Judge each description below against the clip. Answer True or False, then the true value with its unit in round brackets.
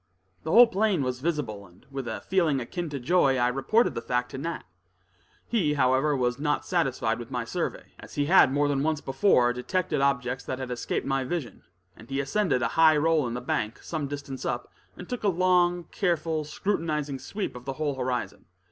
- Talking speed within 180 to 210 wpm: True (200 wpm)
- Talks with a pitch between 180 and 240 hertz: False (145 Hz)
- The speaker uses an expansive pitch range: False (4.7 semitones)